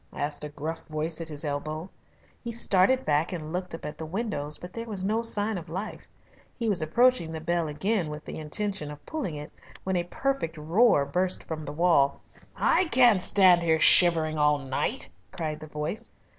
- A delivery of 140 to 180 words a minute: No, average, 195 wpm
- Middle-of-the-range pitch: Yes, medium, 170 Hz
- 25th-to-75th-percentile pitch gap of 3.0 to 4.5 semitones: No, average, 5.1 semitones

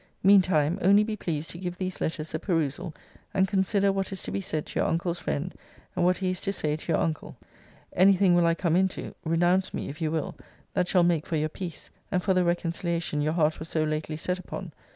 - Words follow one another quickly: Yes, fast, 235 wpm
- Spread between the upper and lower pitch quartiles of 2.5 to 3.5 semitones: Yes, average, 2.9 semitones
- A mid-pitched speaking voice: Yes, medium, 175 Hz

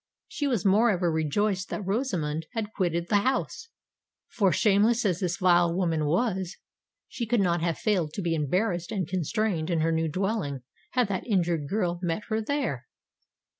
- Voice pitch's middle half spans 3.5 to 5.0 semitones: Yes, average, 4.4 semitones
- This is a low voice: No, medium, 185 Hz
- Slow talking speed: No, average, 165 wpm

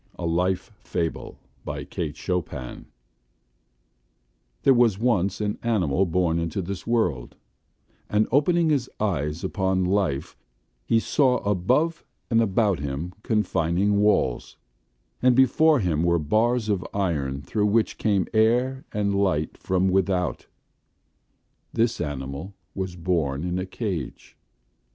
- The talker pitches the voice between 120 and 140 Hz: No, very low, 95 Hz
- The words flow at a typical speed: No, slow, 120 wpm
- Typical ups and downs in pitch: Yes, average, 4.9 semitones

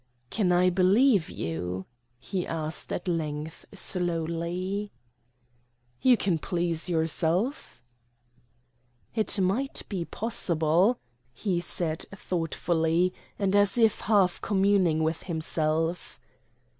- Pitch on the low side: No, medium, 175 Hz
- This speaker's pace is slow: Yes, slow, 95 wpm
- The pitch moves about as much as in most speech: Yes, average, 3.5 semitones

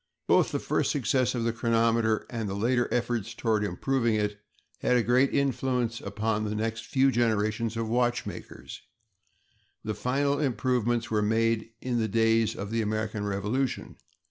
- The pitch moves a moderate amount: No, narrow, 2.1 semitones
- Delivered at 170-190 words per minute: No, average, 155 wpm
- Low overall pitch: Yes, low, 115 Hz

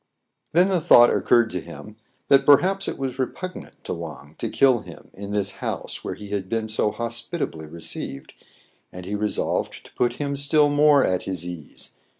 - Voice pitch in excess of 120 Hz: No, low, 115 Hz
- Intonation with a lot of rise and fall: Yes, wide, 7.3 semitones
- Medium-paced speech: Yes, average, 180 wpm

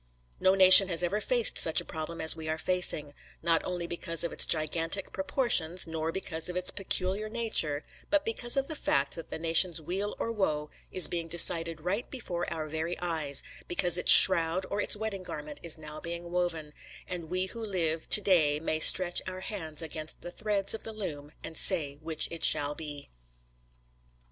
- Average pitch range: Yes, average, 3.1 semitones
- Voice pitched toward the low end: No, medium, 170 Hz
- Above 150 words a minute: Yes, average, 190 wpm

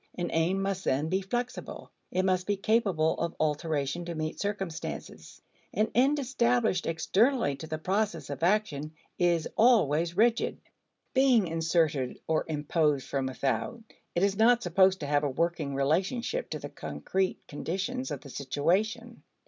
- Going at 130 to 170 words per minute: Yes, average, 150 wpm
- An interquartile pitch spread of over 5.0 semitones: Yes, wide, 5.6 semitones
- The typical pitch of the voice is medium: Yes, medium, 175 Hz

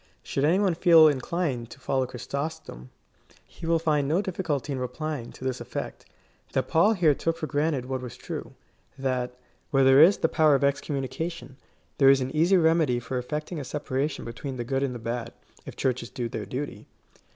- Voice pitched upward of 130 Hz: Yes, medium, 140 Hz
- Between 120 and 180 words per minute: No, average, 195 wpm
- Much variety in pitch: No, average, 3.9 semitones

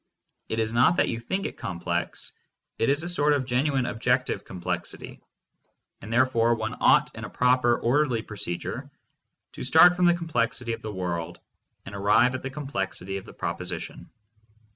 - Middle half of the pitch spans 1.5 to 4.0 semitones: No, average, 4.4 semitones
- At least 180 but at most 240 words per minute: No, average, 165 wpm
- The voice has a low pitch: Yes, low, 120 Hz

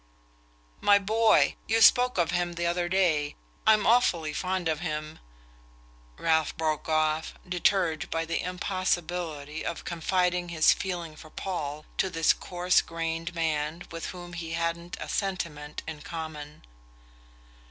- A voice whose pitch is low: No, medium, 165 Hz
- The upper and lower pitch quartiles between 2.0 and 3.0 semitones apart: Yes, narrow, 2.5 semitones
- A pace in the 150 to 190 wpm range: No, slow, 135 wpm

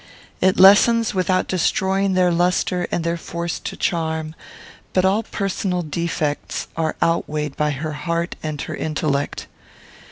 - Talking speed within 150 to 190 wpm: No, slow, 135 wpm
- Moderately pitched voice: Yes, medium, 170 Hz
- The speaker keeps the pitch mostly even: No, average, 3.1 semitones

